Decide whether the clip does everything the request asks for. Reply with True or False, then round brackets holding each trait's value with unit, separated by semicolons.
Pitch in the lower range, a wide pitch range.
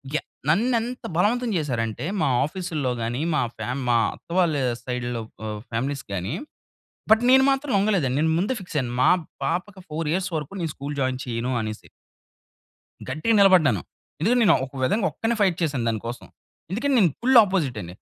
False (155 Hz; 8.1 semitones)